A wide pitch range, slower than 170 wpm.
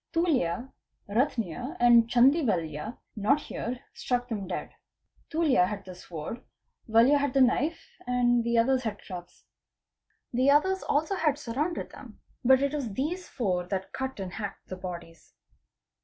Yes: wide, 6.1 semitones; average, 150 wpm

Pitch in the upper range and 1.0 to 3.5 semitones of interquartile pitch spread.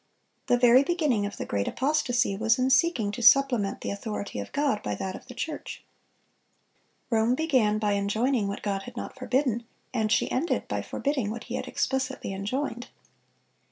No: high, 240 Hz; average, 4.3 semitones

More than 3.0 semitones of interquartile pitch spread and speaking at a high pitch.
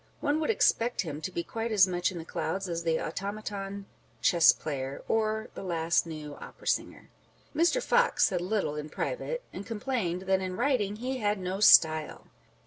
Yes: average, 4.8 semitones; high, 195 Hz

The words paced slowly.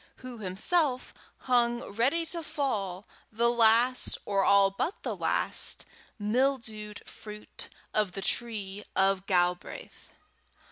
Yes: slow, 110 wpm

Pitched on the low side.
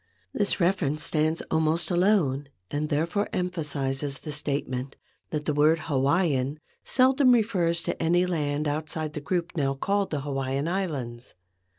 No: medium, 155 Hz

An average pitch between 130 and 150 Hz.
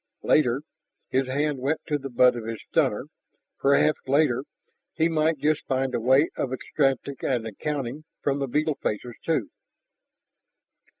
Yes: low, 135 Hz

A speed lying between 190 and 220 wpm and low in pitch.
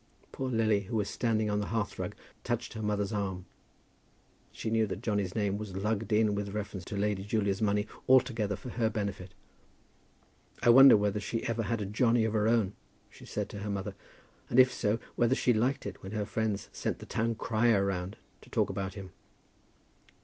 Yes: average, 195 wpm; low, 105 Hz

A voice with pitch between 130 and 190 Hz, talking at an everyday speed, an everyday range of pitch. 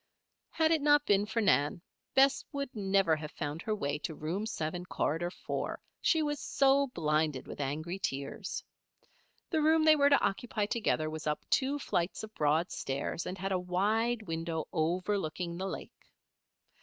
No: medium, 185 Hz; average, 170 wpm; wide, 7.4 semitones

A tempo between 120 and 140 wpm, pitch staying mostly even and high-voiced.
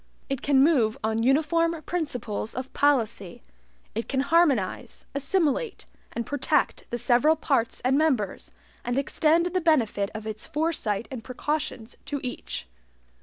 No: slow, 135 wpm; wide, 5.5 semitones; very high, 270 Hz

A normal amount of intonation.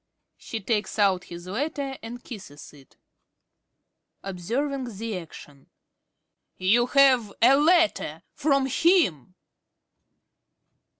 No: wide, 6.9 semitones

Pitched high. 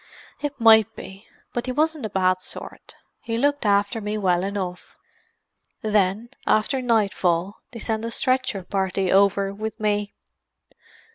Yes: high, 210 Hz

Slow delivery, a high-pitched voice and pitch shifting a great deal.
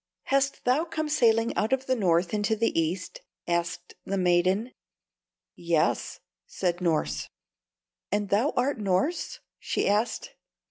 Yes: slow, 130 wpm; high, 205 Hz; wide, 6.2 semitones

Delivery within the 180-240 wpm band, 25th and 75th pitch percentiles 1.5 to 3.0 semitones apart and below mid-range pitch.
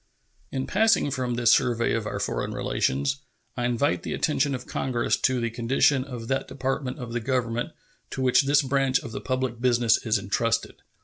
Yes: average, 185 wpm; narrow, 2.4 semitones; low, 125 Hz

